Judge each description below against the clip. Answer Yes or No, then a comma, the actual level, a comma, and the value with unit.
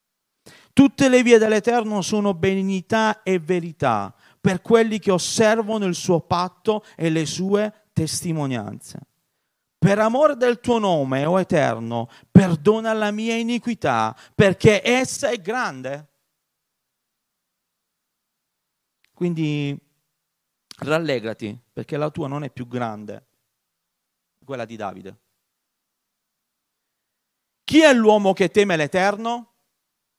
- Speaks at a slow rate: Yes, slow, 105 wpm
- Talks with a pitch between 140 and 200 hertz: Yes, medium, 185 Hz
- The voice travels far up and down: Yes, wide, 7.3 semitones